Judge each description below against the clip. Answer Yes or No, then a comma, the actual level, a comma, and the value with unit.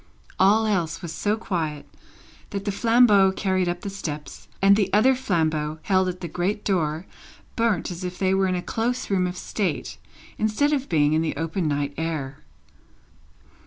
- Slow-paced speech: No, average, 175 wpm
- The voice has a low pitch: No, medium, 185 Hz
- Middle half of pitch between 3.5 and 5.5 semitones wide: Yes, average, 4.2 semitones